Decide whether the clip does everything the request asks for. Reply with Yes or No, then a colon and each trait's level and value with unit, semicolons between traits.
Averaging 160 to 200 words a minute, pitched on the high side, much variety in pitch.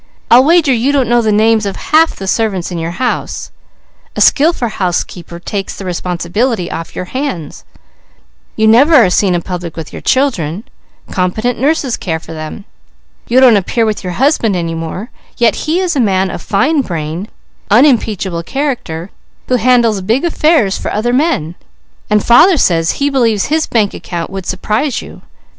Yes: average, 170 wpm; high, 215 Hz; wide, 6.4 semitones